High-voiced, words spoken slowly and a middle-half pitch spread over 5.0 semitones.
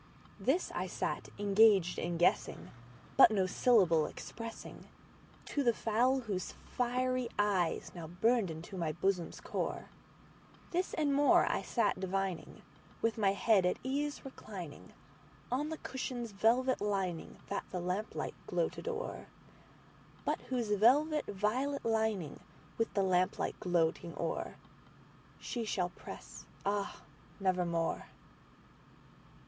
Yes: high, 210 Hz; slow, 110 wpm; wide, 5.5 semitones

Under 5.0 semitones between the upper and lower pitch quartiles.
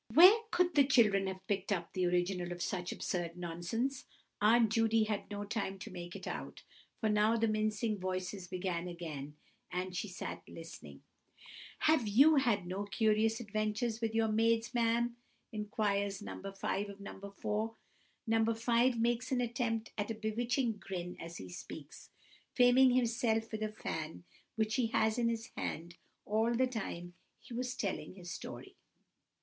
Yes: average, 3.7 semitones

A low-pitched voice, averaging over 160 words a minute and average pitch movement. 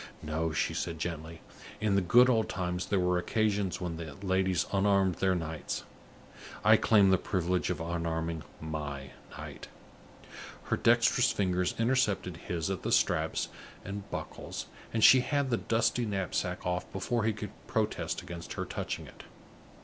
No: very low, 90 Hz; average, 155 wpm; average, 3.6 semitones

